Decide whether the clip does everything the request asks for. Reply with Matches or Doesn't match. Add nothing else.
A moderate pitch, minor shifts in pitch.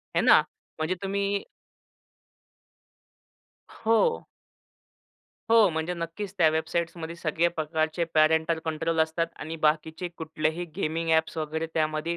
Matches